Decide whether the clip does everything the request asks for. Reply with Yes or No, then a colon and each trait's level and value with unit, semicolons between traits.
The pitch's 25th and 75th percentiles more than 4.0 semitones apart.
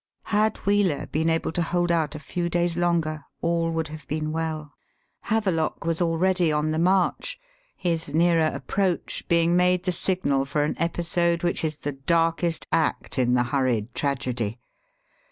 No: narrow, 2.4 semitones